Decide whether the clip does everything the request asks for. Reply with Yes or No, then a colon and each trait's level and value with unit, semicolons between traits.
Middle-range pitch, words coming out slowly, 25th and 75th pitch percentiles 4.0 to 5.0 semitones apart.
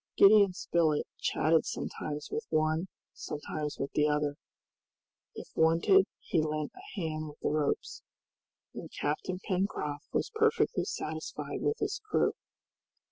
Yes: medium, 160 Hz; slow, 130 wpm; average, 4.5 semitones